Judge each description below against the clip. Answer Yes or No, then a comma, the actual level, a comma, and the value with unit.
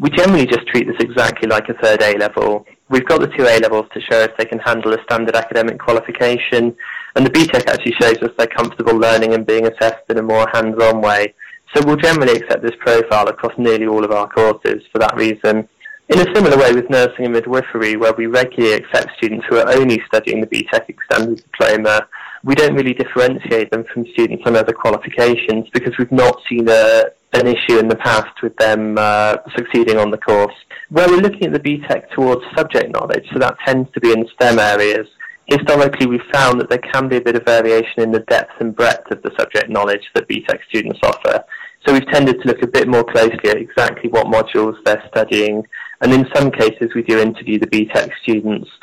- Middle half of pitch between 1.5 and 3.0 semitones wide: Yes, narrow, 2.4 semitones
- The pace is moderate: No, fast, 215 wpm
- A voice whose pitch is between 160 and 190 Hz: No, low, 115 Hz